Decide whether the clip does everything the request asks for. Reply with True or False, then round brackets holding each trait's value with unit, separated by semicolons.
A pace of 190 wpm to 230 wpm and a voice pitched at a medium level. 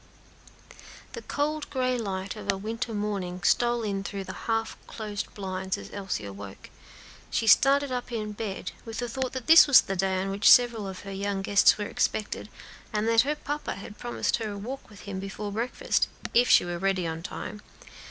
False (200 wpm; 210 Hz)